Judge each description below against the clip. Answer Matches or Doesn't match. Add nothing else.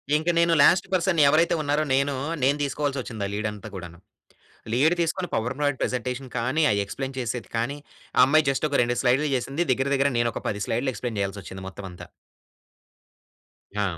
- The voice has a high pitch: Doesn't match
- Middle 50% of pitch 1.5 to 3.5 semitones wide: Doesn't match